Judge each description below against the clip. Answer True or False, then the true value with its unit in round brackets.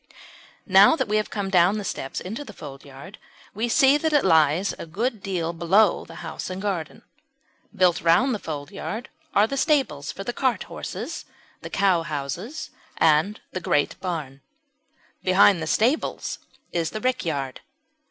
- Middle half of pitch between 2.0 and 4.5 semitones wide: False (5.1 semitones)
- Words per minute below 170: True (155 wpm)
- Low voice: False (185 Hz)